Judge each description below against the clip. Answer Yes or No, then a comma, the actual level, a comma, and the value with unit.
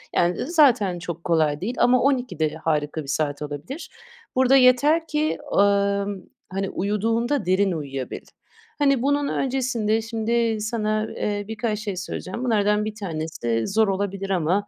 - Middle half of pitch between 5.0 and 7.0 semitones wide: Yes, average, 5.3 semitones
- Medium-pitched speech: No, high, 210 Hz